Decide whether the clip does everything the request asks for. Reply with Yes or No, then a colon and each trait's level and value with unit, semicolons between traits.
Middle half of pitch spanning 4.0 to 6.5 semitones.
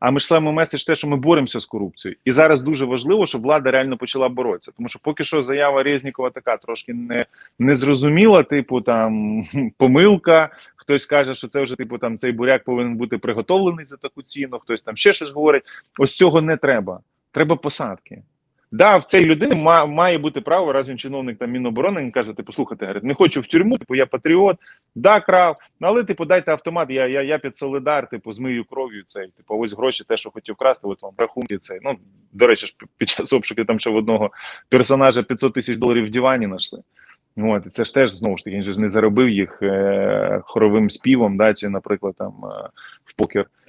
Yes: average, 4.6 semitones